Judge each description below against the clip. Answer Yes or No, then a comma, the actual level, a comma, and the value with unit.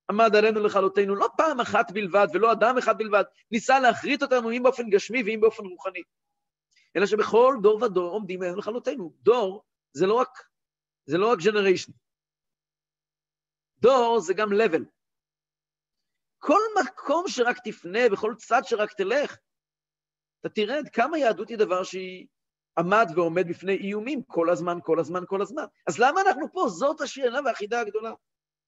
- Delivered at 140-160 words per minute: Yes, fast, 150 wpm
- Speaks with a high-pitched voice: Yes, high, 215 Hz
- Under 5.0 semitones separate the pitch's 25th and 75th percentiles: No, average, 5.3 semitones